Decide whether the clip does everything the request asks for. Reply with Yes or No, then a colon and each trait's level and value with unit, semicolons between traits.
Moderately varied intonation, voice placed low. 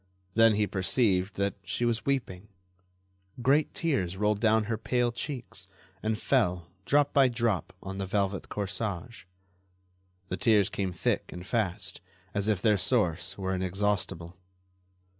Yes: average, 3.8 semitones; low, 105 Hz